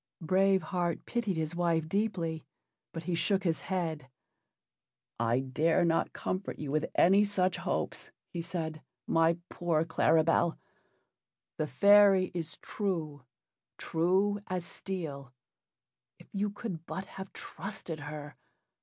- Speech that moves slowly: Yes, slow, 125 wpm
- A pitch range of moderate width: Yes, average, 3.3 semitones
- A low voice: No, medium, 170 Hz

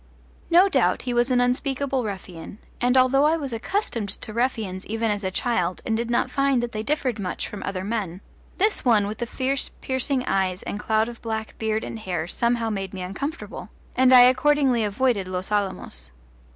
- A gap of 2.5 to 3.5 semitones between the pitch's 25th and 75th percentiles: No, average, 4.3 semitones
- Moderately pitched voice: No, high, 230 Hz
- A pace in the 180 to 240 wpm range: Yes, average, 190 wpm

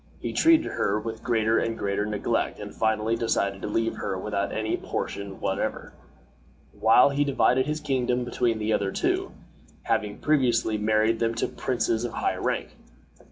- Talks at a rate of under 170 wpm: Yes, average, 160 wpm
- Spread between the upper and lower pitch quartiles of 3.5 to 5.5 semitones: No, narrow, 2.4 semitones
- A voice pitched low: Yes, low, 115 Hz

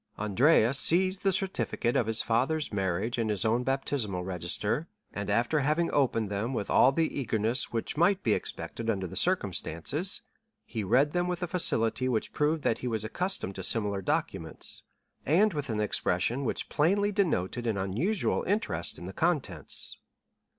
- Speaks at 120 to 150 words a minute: No, average, 165 wpm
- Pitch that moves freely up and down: Yes, wide, 7.4 semitones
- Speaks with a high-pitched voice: No, low, 120 Hz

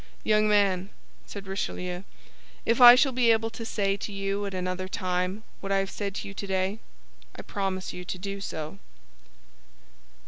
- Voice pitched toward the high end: Yes, high, 195 Hz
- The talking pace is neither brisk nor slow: Yes, average, 170 wpm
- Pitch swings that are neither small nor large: No, narrow, 2.2 semitones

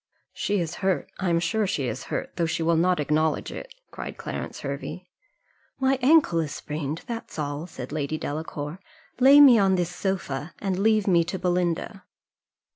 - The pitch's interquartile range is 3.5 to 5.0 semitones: Yes, average, 4.2 semitones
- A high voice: No, medium, 175 Hz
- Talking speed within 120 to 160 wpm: No, average, 175 wpm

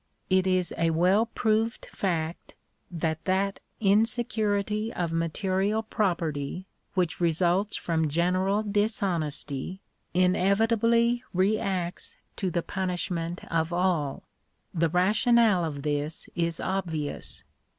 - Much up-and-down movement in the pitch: No, average, 3.7 semitones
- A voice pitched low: No, medium, 185 Hz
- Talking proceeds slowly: Yes, slow, 100 wpm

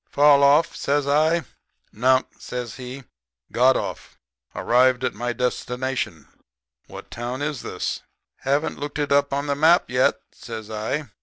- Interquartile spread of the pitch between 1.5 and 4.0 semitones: Yes, average, 2.7 semitones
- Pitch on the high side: No, low, 130 Hz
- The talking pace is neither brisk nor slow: Yes, average, 145 wpm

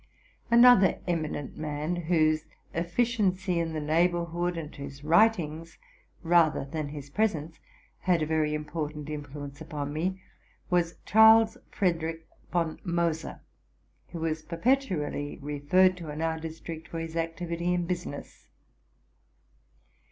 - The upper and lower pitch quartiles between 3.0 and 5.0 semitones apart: No, narrow, 2.5 semitones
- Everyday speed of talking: No, slow, 125 wpm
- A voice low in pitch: No, medium, 165 Hz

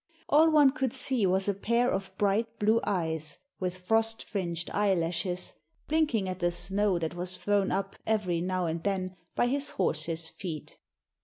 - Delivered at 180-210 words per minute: No, average, 165 wpm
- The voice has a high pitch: Yes, high, 195 Hz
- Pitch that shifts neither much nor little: Yes, average, 4.2 semitones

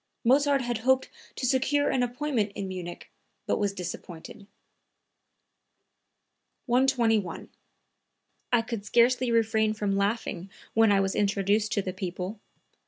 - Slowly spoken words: Yes, slow, 120 wpm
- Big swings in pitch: No, average, 3.9 semitones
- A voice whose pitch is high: Yes, high, 220 Hz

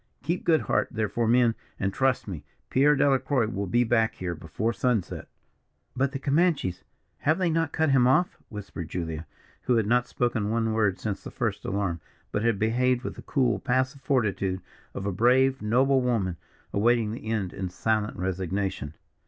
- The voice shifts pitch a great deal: No, average, 4.8 semitones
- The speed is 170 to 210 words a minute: Yes, average, 175 wpm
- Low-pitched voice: Yes, low, 115 Hz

